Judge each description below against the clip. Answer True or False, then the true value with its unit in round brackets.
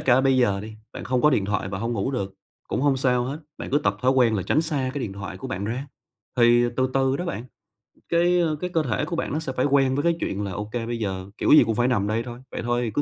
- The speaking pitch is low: True (125 Hz)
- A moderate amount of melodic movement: True (4.3 semitones)